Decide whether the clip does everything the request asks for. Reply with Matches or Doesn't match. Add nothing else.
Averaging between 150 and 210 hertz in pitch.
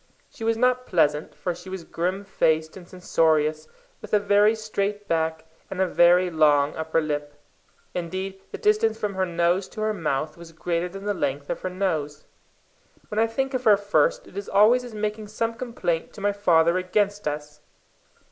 Matches